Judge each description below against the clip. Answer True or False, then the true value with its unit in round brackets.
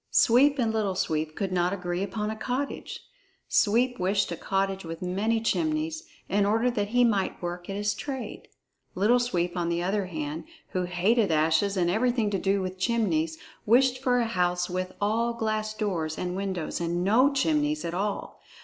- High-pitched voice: True (195 Hz)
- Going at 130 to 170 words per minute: False (180 wpm)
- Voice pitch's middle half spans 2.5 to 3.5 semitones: False (4.4 semitones)